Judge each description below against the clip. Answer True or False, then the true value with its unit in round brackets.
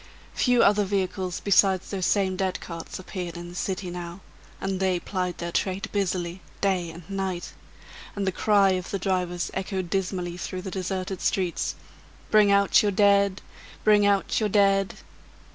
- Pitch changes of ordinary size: False (1.8 semitones)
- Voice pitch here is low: False (190 Hz)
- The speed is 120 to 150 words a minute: False (160 wpm)